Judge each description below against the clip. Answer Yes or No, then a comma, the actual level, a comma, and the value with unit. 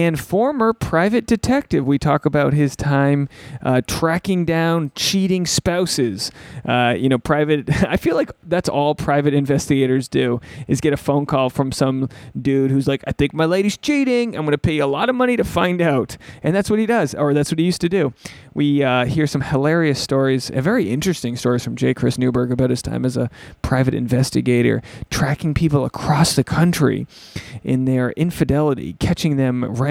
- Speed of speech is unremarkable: Yes, average, 195 wpm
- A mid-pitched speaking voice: Yes, medium, 145 Hz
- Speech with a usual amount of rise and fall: Yes, average, 4.3 semitones